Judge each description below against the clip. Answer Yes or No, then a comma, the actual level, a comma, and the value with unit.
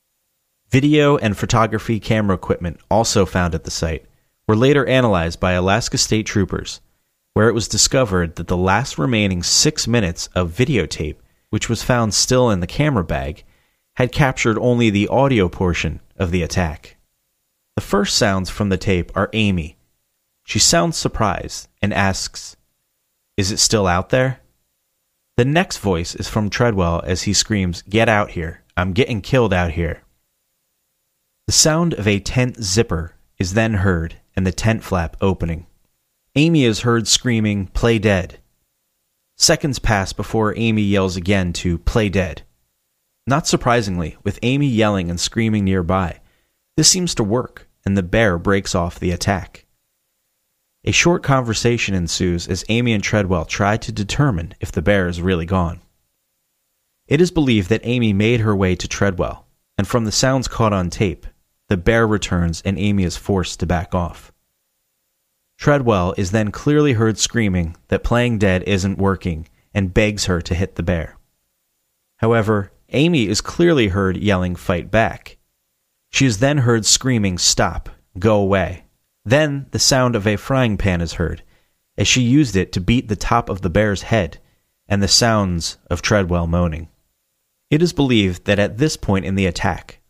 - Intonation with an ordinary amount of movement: Yes, average, 4.5 semitones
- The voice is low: Yes, low, 100 Hz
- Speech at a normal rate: Yes, average, 160 wpm